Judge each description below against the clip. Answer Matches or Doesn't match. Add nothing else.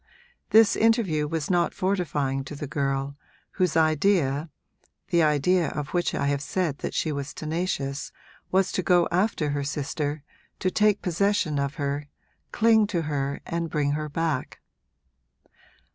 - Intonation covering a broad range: Doesn't match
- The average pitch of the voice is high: Doesn't match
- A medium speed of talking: Matches